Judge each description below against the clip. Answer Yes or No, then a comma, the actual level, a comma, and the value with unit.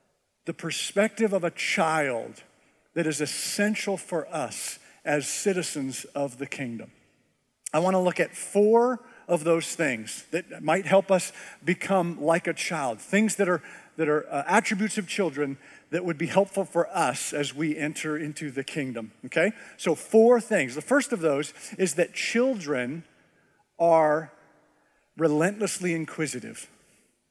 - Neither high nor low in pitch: Yes, medium, 170 Hz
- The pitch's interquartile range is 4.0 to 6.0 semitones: Yes, average, 4.6 semitones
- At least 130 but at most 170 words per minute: Yes, average, 145 wpm